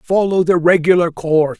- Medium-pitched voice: Yes, medium, 170 Hz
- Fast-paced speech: No, average, 150 wpm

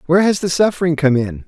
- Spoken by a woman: No, male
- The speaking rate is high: Yes, fast, 245 wpm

